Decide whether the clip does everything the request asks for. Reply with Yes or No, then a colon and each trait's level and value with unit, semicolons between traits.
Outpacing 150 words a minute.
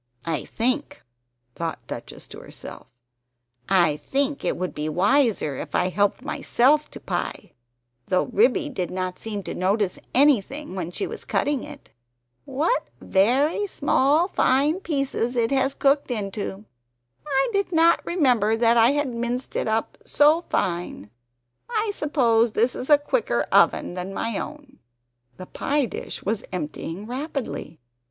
No: average, 145 wpm